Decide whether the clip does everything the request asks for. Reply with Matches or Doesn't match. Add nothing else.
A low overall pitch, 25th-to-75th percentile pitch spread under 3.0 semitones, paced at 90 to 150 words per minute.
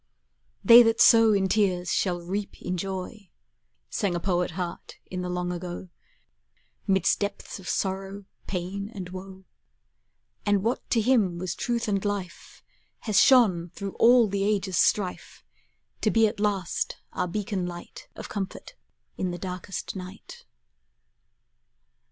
Doesn't match